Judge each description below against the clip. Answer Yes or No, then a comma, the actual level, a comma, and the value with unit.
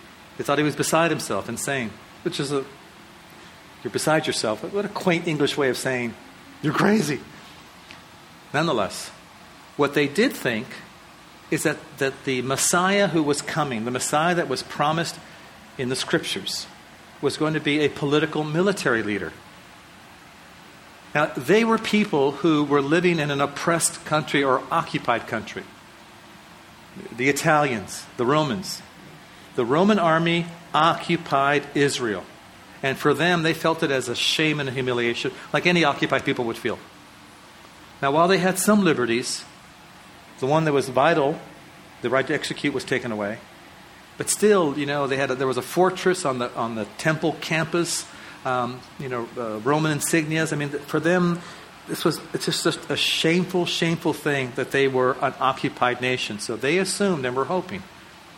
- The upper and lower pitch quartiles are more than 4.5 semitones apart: No, average, 4.0 semitones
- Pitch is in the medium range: Yes, medium, 150 Hz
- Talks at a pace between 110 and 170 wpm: Yes, average, 165 wpm